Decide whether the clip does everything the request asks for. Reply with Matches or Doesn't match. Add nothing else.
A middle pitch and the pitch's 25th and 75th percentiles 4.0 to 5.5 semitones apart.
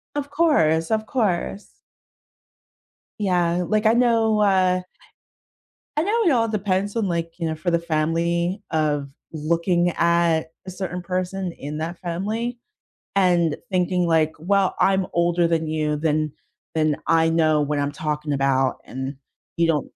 Doesn't match